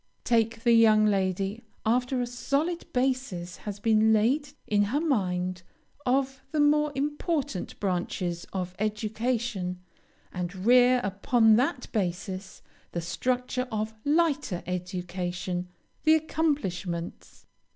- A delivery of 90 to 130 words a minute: Yes, slow, 110 wpm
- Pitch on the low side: No, high, 220 Hz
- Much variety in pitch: Yes, wide, 5.7 semitones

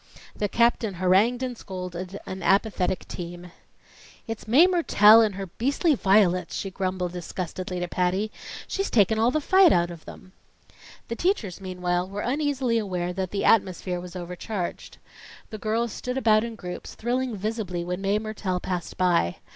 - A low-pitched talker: No, high, 195 Hz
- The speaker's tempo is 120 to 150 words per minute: No, average, 160 wpm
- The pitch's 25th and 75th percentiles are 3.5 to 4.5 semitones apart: Yes, average, 4.0 semitones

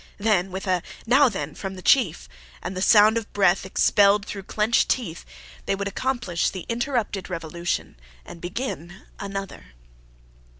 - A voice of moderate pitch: No, high, 195 Hz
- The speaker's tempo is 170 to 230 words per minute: No, average, 155 wpm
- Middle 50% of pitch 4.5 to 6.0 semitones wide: No, average, 3.8 semitones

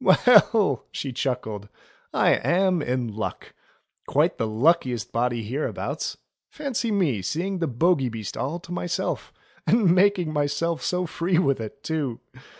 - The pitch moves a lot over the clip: Yes, wide, 6.7 semitones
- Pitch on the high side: No, medium, 155 Hz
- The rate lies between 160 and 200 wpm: No, average, 145 wpm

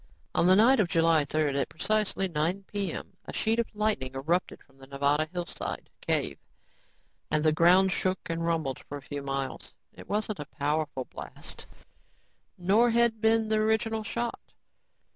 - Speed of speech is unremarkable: Yes, average, 160 wpm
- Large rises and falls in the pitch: Yes, wide, 6.5 semitones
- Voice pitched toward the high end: No, medium, 175 Hz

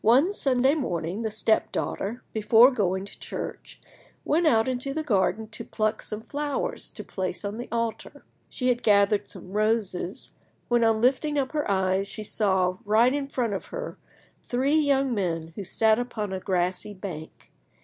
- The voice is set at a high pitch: Yes, high, 220 Hz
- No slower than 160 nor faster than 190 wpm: Yes, average, 170 wpm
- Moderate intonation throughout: Yes, average, 4.6 semitones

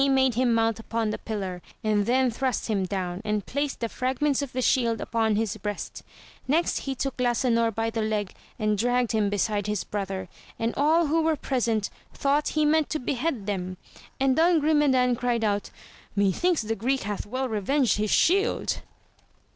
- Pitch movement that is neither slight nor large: Yes, average, 4.3 semitones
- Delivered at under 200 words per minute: Yes, average, 180 wpm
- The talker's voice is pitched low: No, high, 230 Hz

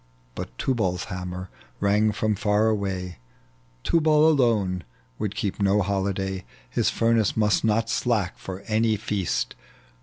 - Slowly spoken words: Yes, slow, 125 wpm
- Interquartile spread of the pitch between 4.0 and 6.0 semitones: No, average, 2.8 semitones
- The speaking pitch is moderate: No, low, 105 Hz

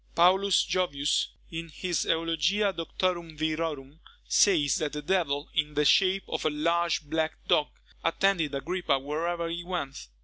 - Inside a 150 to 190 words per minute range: No, average, 140 wpm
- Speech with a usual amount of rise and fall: Yes, average, 3.0 semitones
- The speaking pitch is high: No, medium, 165 Hz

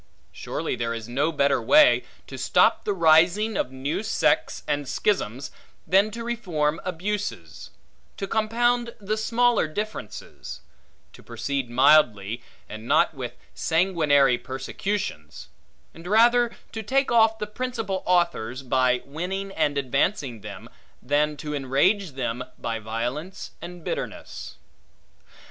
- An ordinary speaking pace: No, slow, 125 wpm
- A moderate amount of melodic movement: No, wide, 8.1 semitones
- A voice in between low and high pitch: Yes, medium, 160 Hz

